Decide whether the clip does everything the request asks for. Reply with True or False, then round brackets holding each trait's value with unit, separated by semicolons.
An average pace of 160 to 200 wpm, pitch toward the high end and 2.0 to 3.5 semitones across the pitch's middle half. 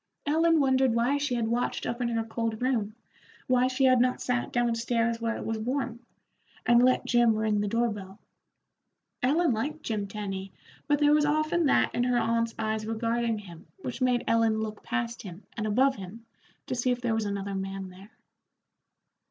True (190 wpm; 235 Hz; 2.6 semitones)